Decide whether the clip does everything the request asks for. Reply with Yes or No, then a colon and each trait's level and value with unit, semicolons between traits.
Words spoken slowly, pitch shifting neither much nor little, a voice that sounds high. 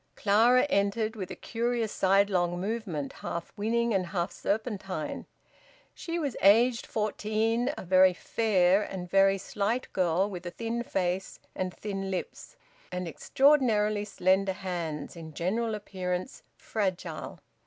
Yes: slow, 130 wpm; average, 3.6 semitones; high, 200 Hz